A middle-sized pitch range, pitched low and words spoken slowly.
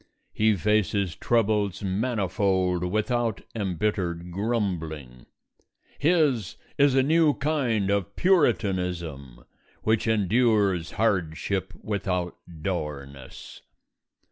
Yes: average, 4.3 semitones; low, 100 Hz; slow, 80 wpm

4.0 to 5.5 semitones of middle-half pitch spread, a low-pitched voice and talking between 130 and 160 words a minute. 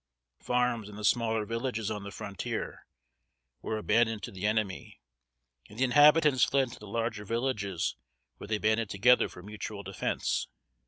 No: average, 2.9 semitones; low, 110 Hz; average, 155 wpm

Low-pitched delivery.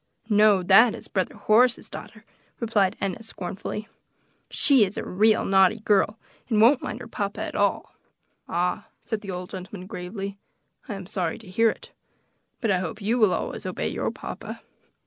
No: high, 205 Hz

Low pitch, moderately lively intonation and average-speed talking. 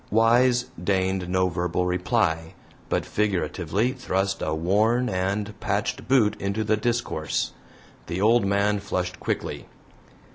No: low, 100 Hz; average, 3.5 semitones; slow, 120 wpm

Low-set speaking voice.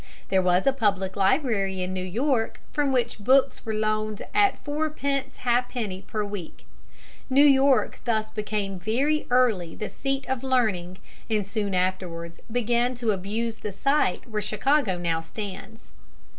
No: high, 220 Hz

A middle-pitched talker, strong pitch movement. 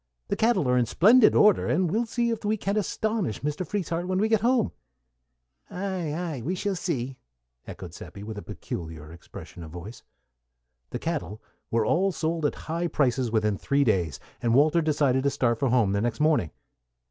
Yes: medium, 150 Hz; wide, 8.5 semitones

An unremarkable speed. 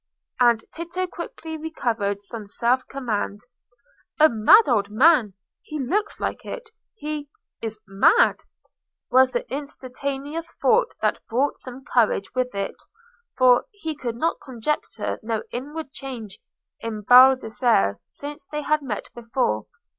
No: slow, 120 wpm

